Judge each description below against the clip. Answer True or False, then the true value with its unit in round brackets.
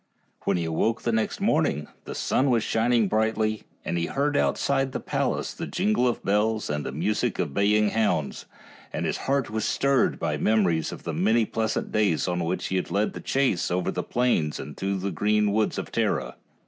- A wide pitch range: False (4.2 semitones)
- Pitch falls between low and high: False (105 Hz)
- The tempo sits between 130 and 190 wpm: False (200 wpm)